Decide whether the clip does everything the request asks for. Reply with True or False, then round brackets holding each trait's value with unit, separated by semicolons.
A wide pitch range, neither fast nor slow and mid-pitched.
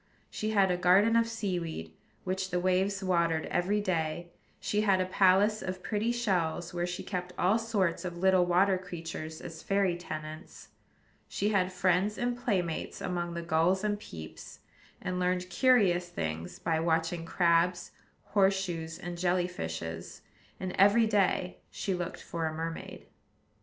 False (2.6 semitones; 155 wpm; 180 Hz)